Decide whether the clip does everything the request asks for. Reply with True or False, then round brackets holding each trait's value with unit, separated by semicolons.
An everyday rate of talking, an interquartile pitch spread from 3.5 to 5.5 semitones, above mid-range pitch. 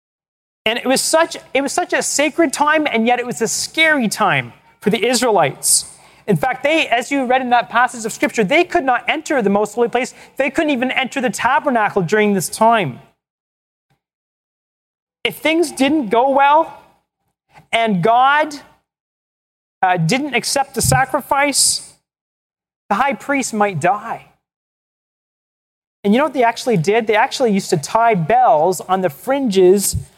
True (160 wpm; 4.7 semitones; 245 Hz)